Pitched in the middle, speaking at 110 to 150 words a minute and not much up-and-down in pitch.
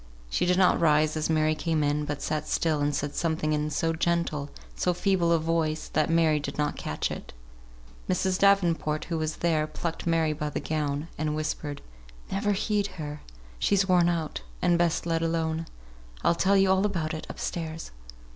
No: medium, 160 Hz; average, 185 wpm; narrow, 2.1 semitones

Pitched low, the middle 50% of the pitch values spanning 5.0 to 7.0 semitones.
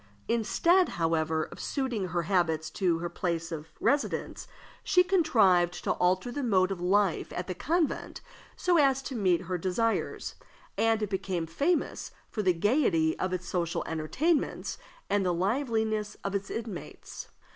No: high, 190 Hz; wide, 5.6 semitones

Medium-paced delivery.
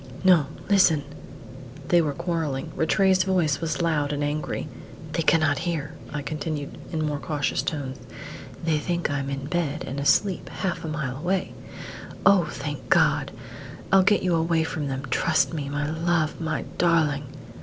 Yes: average, 155 wpm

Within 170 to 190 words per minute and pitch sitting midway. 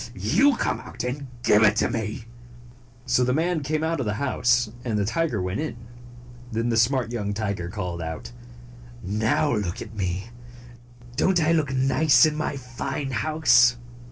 No: average, 175 wpm; low, 120 Hz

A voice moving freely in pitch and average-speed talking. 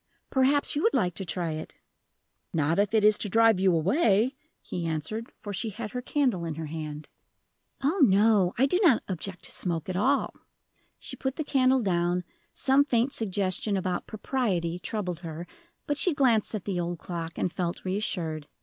Yes: wide, 6.1 semitones; average, 185 wpm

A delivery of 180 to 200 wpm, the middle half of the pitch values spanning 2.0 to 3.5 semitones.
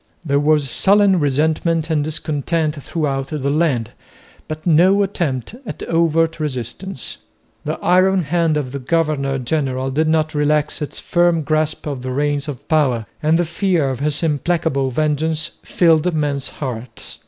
No: average, 150 wpm; average, 2.9 semitones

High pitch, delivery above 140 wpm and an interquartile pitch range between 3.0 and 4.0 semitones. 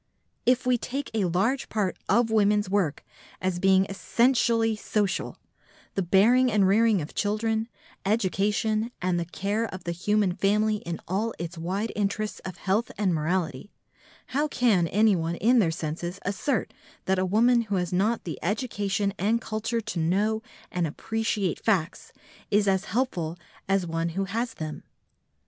Yes: high, 200 Hz; average, 155 wpm; average, 3.5 semitones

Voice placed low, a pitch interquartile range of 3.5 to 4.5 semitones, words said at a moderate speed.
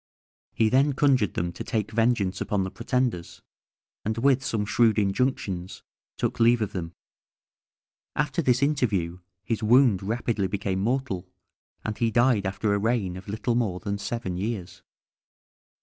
Yes: low, 110 Hz; average, 4.0 semitones; average, 150 wpm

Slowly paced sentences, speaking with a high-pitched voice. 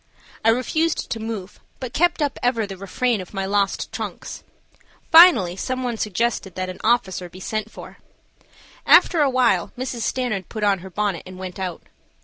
No: average, 170 wpm; high, 215 Hz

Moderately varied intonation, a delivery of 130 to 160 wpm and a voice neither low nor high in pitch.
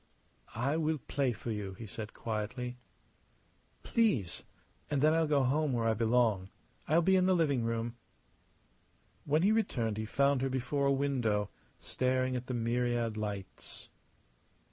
No: average, 3.9 semitones; average, 150 wpm; low, 125 Hz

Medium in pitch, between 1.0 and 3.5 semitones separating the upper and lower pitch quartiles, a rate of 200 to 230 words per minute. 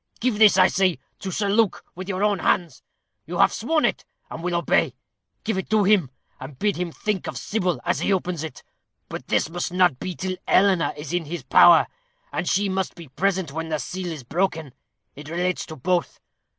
Yes: medium, 180 Hz; average, 3.0 semitones; fast, 205 wpm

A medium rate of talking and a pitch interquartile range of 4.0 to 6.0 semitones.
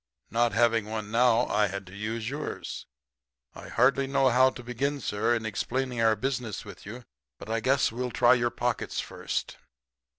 No: average, 175 wpm; narrow, 2.6 semitones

